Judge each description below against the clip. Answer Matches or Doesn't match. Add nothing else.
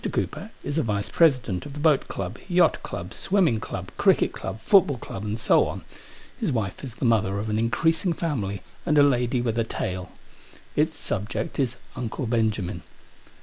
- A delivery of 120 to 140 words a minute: Doesn't match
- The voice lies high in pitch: Doesn't match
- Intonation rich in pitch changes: Matches